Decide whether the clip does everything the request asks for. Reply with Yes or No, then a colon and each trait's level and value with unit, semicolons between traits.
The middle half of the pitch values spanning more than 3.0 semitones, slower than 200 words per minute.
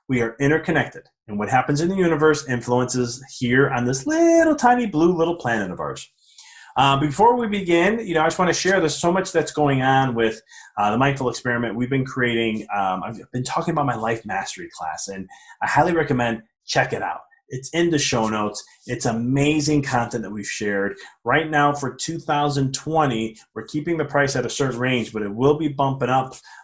No: average, 4.6 semitones; fast, 205 wpm